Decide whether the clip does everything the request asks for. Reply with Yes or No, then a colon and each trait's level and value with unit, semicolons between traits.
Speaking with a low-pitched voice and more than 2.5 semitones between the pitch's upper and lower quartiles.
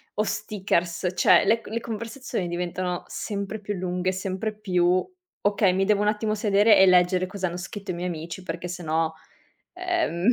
No: high, 190 Hz; average, 2.9 semitones